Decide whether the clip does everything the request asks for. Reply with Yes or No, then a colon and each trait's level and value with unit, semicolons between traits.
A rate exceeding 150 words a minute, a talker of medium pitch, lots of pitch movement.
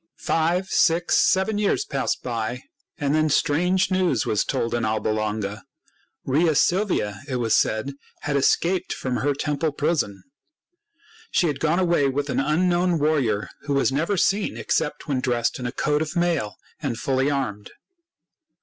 Yes: average, 160 wpm; medium, 145 Hz; wide, 5.8 semitones